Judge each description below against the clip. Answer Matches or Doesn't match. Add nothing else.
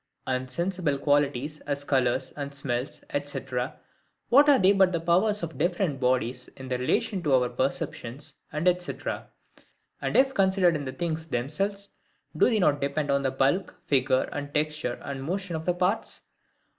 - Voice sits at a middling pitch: Matches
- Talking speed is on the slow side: Doesn't match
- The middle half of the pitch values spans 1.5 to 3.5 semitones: Doesn't match